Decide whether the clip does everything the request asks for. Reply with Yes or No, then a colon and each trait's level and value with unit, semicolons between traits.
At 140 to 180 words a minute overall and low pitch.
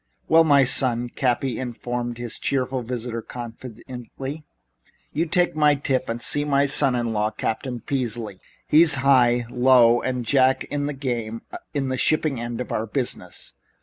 Yes: average, 155 wpm; low, 125 Hz